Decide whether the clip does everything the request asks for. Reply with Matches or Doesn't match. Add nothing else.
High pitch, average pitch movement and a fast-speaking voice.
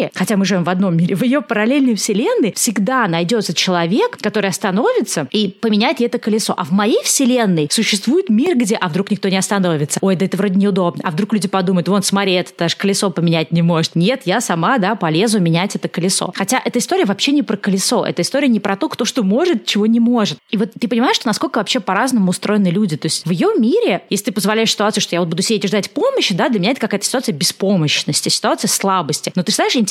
Matches